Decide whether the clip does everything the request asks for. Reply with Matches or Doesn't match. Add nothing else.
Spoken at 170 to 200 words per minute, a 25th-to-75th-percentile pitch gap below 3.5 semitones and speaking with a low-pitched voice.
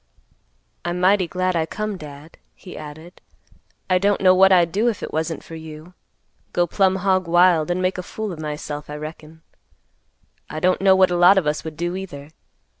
Doesn't match